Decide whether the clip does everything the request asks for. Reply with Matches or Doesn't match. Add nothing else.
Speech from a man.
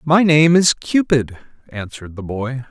Matches